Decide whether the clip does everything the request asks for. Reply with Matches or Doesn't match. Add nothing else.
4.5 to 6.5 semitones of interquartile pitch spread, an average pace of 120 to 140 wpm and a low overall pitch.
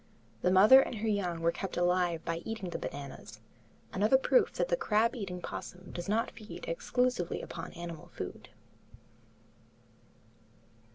Doesn't match